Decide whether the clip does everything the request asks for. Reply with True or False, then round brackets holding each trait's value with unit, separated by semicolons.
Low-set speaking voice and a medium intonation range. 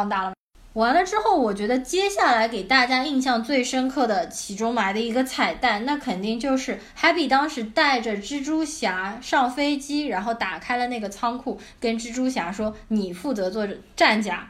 False (245 Hz; 3.9 semitones)